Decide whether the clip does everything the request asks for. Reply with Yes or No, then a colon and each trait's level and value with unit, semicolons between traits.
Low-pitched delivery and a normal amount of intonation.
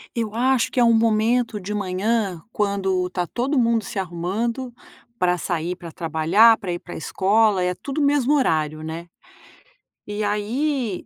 No: high, 210 Hz; average, 4.5 semitones